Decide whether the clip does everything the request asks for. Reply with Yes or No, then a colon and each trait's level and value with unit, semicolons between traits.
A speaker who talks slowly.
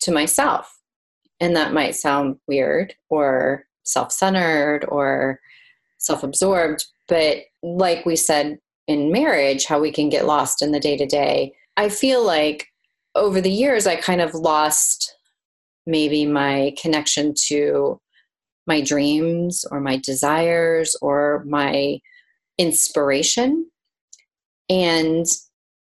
Yes: slow, 115 wpm